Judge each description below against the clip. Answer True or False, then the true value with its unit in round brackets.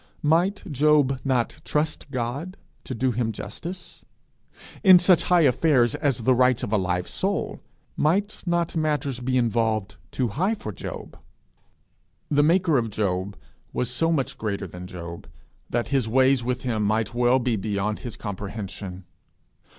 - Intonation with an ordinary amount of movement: False (5.8 semitones)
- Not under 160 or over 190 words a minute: False (150 wpm)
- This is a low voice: True (125 Hz)